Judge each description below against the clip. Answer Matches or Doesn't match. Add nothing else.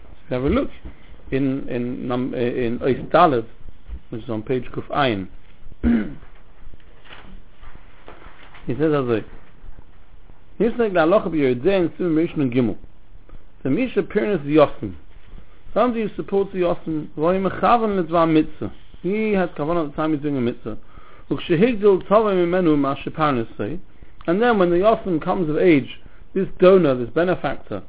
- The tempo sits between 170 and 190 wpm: Doesn't match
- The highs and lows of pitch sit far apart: Matches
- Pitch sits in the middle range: Matches